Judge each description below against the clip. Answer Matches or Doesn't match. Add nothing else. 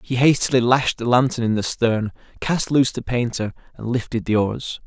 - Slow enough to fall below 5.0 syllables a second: Doesn't match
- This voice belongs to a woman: Doesn't match